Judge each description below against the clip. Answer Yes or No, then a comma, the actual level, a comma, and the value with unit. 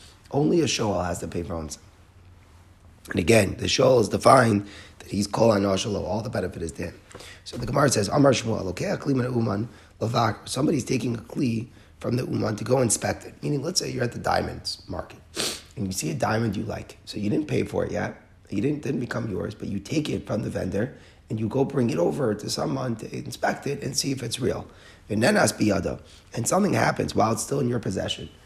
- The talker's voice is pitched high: No, low, 105 Hz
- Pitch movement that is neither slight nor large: Yes, average, 3.9 semitones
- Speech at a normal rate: No, fast, 215 wpm